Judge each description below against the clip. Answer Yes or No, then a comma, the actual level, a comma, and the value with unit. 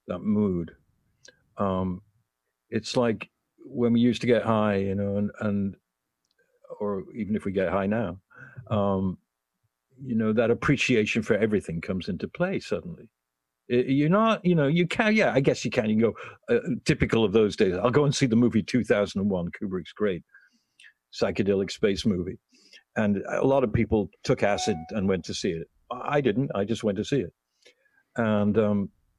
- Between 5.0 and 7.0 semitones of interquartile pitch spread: No, average, 4.1 semitones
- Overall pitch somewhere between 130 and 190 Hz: No, low, 105 Hz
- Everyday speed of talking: Yes, average, 180 wpm